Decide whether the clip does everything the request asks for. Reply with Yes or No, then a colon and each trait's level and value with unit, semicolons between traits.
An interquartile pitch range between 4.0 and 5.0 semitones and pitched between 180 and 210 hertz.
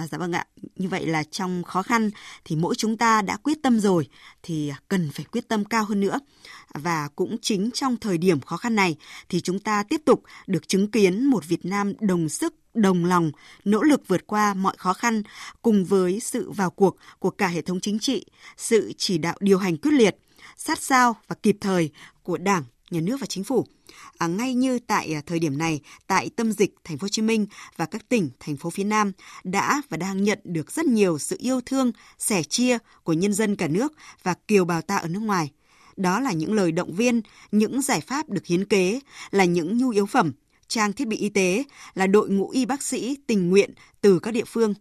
Yes: average, 4.5 semitones; high, 200 Hz